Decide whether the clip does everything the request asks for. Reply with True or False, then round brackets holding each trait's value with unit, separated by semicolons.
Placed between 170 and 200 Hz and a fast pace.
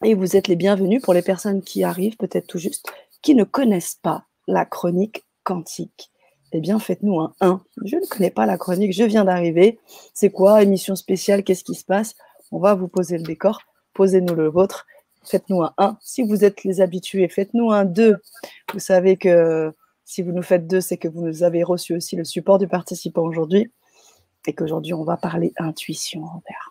False (190 Hz; 200 wpm)